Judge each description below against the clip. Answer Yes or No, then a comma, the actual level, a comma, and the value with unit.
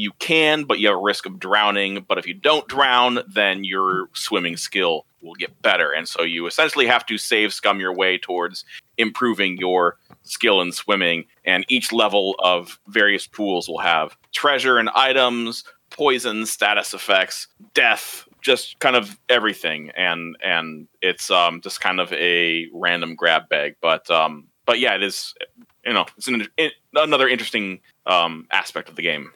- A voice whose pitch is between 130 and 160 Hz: No, low, 100 Hz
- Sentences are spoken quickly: No, average, 175 wpm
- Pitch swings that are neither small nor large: No, wide, 5.8 semitones